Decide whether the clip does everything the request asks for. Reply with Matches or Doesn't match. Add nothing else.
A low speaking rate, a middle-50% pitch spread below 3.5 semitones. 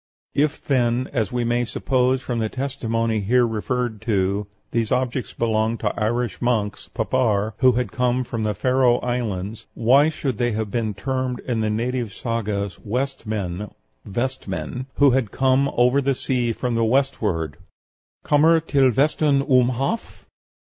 Doesn't match